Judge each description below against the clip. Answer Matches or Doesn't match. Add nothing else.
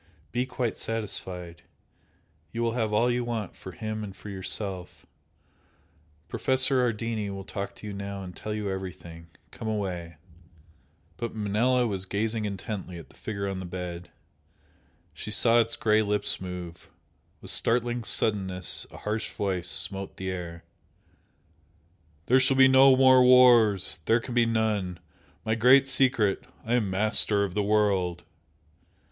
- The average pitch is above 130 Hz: Doesn't match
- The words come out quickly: Doesn't match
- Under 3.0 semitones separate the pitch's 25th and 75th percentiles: Doesn't match